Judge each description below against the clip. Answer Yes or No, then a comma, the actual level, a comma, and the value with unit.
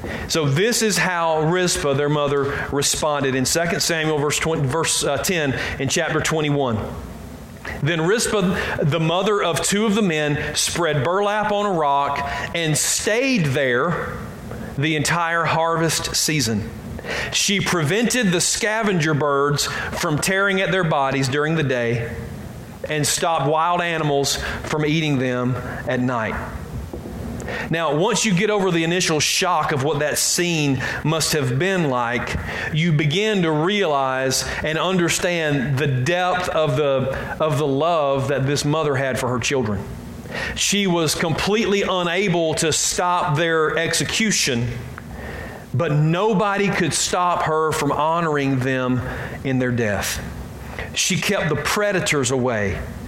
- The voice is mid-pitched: Yes, medium, 155 Hz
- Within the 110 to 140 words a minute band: Yes, slow, 135 wpm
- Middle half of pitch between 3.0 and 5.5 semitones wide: Yes, average, 4.4 semitones